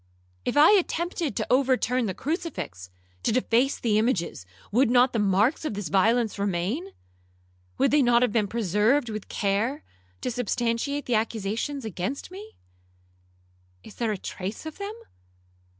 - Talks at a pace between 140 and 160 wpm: Yes, average, 150 wpm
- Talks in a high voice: Yes, high, 235 Hz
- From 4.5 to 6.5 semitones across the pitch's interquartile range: Yes, average, 5.2 semitones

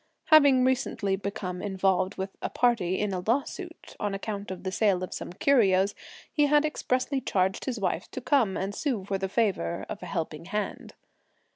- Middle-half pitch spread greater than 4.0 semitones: Yes, average, 5.2 semitones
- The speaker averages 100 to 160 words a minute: No, average, 180 wpm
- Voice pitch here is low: No, high, 200 Hz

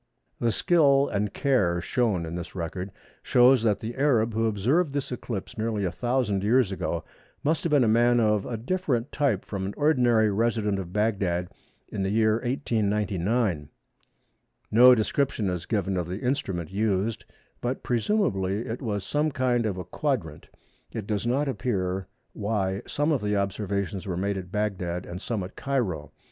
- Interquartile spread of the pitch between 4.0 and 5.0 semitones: Yes, average, 4.4 semitones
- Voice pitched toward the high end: No, low, 110 Hz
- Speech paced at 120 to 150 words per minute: No, average, 170 wpm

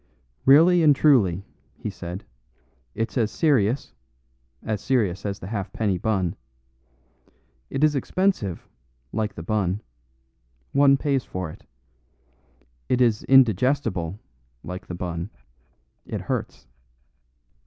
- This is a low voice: Yes, low, 110 Hz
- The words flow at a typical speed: No, slow, 110 wpm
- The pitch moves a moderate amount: No, wide, 6.7 semitones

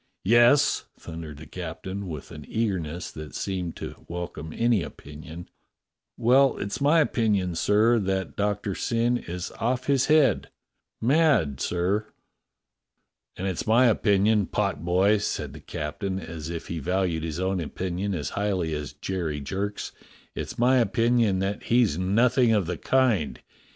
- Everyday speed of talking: Yes, average, 150 wpm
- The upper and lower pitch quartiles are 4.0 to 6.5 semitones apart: Yes, average, 5.3 semitones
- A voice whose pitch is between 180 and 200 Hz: No, very low, 95 Hz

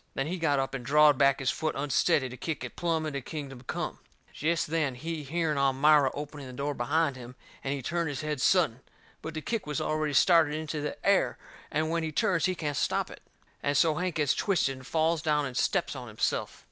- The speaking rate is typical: No, fast, 225 wpm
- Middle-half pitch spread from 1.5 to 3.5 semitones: Yes, average, 2.8 semitones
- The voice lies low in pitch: No, medium, 150 Hz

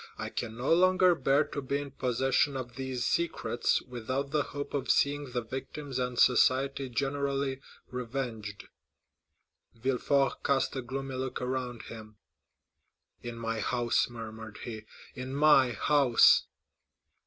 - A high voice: No, low, 130 Hz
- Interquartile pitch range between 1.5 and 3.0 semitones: Yes, narrow, 2.4 semitones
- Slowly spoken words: Yes, slow, 130 wpm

